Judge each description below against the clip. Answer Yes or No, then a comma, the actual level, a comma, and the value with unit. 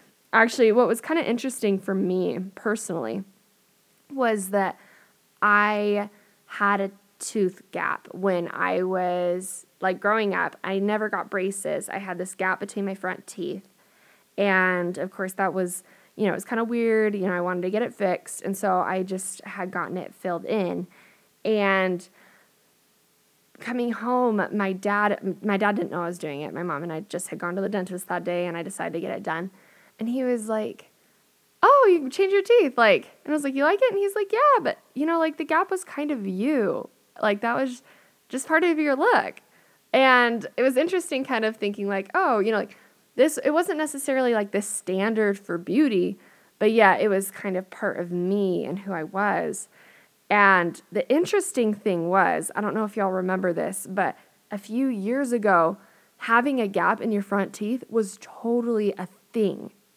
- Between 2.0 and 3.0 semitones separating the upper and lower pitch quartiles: No, average, 4.0 semitones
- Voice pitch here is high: Yes, high, 205 Hz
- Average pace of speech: Yes, average, 195 wpm